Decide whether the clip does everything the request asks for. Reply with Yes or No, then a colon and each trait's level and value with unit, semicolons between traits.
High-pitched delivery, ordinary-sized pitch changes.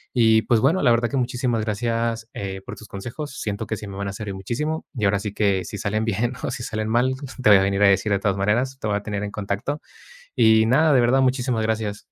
No: low, 110 Hz; average, 3.0 semitones